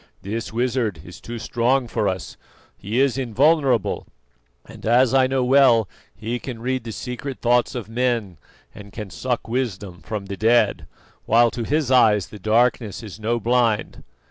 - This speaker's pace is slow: No, average, 165 wpm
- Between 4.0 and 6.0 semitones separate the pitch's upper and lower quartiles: No, average, 3.0 semitones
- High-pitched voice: No, low, 115 Hz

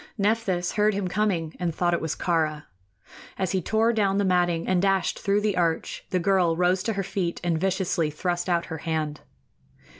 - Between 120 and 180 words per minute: No, average, 190 wpm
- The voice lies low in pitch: No, medium, 180 Hz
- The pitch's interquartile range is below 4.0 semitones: Yes, average, 2.7 semitones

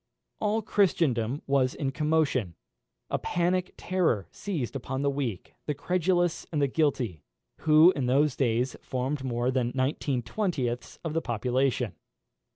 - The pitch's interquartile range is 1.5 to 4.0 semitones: No, average, 4.6 semitones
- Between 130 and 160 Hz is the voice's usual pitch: Yes, medium, 140 Hz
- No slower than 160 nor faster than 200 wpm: No, average, 140 wpm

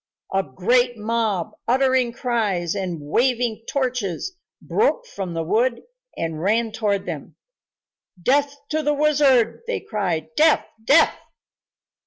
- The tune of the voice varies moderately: No, wide, 5.9 semitones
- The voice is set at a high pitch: Yes, high, 230 Hz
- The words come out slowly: Yes, slow, 120 wpm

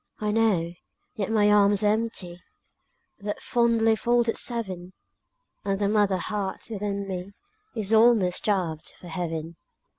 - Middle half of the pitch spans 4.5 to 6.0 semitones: No, average, 3.2 semitones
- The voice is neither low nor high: No, high, 205 Hz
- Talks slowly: Yes, slow, 130 wpm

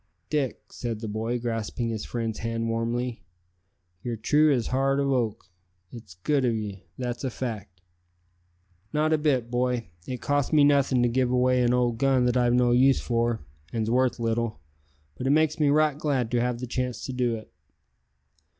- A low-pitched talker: Yes, low, 125 Hz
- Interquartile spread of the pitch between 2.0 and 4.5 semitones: Yes, narrow, 2.4 semitones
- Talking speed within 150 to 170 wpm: No, average, 185 wpm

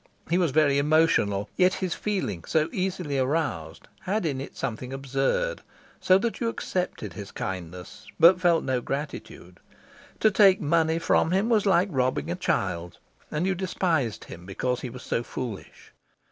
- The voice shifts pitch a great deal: Yes, wide, 6.8 semitones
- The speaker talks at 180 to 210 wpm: No, average, 160 wpm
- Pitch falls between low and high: Yes, medium, 150 Hz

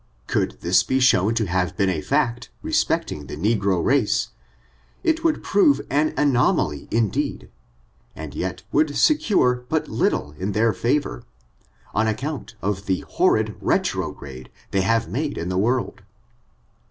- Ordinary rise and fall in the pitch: No, wide, 6.6 semitones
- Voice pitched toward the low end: Yes, low, 115 Hz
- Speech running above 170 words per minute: No, average, 150 wpm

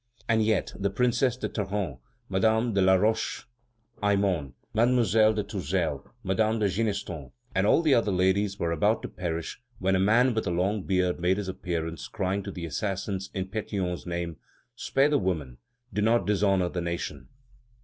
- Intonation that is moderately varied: Yes, average, 3.3 semitones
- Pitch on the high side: No, very low, 95 Hz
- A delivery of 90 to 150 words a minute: No, average, 170 wpm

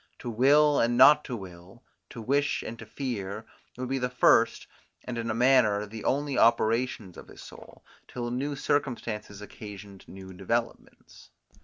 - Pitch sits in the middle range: No, low, 115 Hz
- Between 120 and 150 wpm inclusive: No, average, 160 wpm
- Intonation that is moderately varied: Yes, average, 3.8 semitones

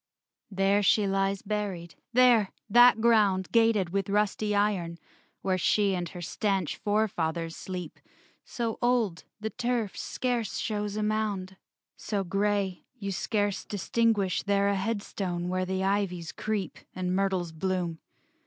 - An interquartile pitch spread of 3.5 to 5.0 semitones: No, narrow, 2.4 semitones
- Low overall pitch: No, high, 200 Hz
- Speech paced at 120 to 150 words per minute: Yes, slow, 135 wpm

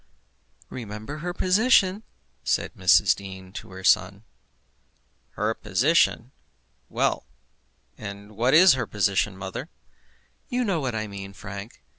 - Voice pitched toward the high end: No, low, 110 Hz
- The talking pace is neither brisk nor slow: No, slow, 120 wpm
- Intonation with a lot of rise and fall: Yes, wide, 8.2 semitones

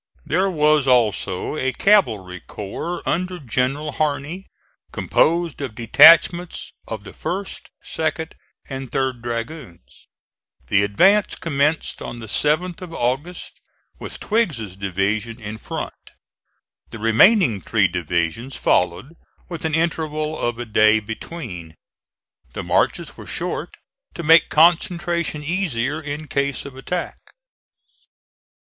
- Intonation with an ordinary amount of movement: No, wide, 6.9 semitones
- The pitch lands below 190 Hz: Yes, medium, 140 Hz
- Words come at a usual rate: No, slow, 115 wpm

